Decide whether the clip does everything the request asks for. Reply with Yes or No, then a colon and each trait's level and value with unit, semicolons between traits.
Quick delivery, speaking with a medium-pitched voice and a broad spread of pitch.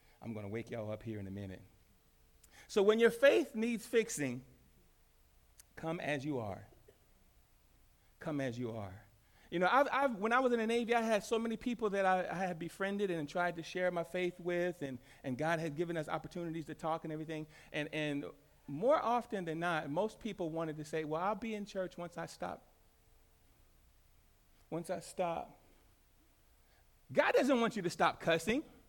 No: average, 190 wpm; medium, 165 Hz; wide, 8.8 semitones